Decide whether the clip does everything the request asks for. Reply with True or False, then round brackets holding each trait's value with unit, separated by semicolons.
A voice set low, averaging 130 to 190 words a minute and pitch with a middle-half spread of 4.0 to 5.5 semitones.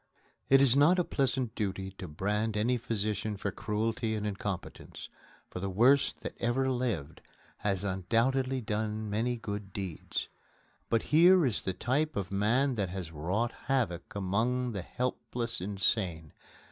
True (110 Hz; 145 wpm; 4.4 semitones)